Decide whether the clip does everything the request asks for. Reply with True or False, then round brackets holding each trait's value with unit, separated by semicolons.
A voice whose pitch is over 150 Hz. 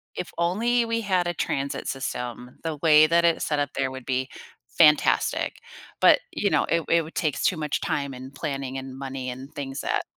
False (145 Hz)